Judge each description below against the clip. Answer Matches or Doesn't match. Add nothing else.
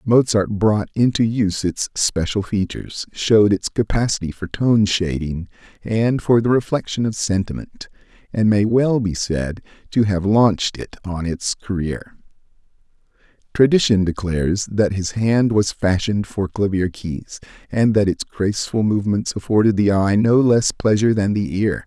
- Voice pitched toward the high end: Doesn't match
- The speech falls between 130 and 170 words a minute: Matches